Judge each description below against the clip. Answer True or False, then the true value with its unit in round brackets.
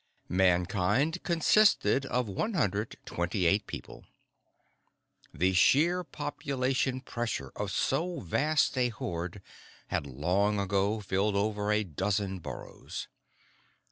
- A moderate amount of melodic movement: False (6.1 semitones)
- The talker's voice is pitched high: False (105 Hz)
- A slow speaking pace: True (100 wpm)